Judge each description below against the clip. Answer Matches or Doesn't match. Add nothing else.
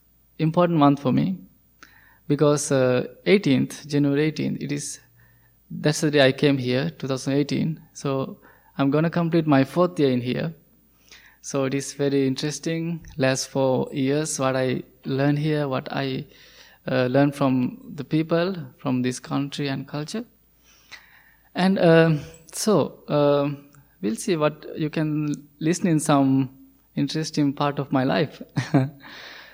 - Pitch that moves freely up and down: Doesn't match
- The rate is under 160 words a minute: Matches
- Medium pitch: Matches